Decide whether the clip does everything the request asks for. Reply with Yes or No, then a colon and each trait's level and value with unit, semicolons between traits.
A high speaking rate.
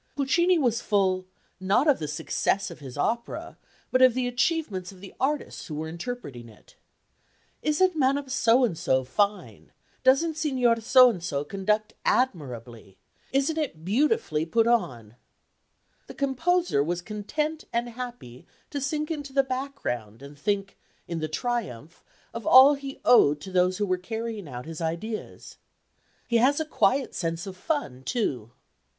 No: average, 155 wpm